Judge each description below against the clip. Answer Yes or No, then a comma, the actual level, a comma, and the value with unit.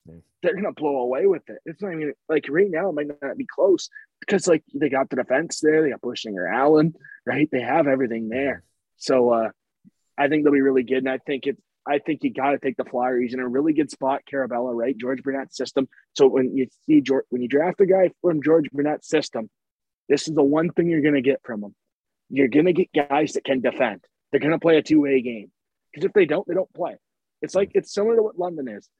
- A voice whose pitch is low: No, medium, 145 Hz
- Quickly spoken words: Yes, fast, 240 wpm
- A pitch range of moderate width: Yes, average, 3.8 semitones